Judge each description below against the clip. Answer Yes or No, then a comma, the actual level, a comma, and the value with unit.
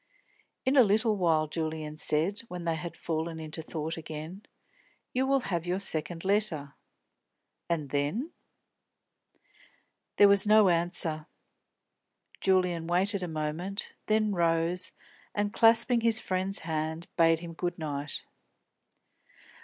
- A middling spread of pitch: Yes, average, 4.0 semitones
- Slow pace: Yes, slow, 120 wpm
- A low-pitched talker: No, medium, 170 Hz